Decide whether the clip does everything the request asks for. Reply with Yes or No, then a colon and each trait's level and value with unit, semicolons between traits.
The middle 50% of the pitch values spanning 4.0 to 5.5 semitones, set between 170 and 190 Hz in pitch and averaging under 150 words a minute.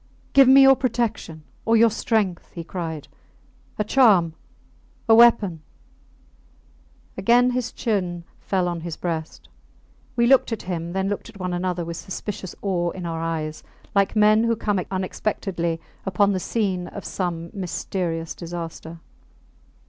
Yes: average, 4.4 semitones; medium, 185 Hz; average, 140 wpm